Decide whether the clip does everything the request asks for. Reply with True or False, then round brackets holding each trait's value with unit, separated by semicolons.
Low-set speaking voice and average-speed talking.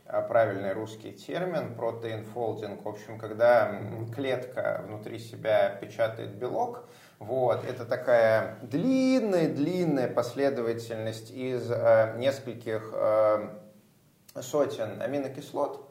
False (115 Hz; 85 wpm)